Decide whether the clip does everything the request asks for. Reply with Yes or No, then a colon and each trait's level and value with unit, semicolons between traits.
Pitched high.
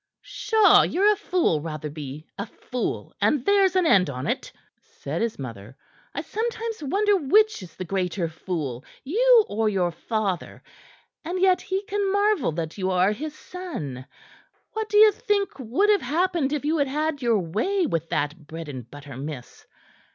Yes: high, 245 Hz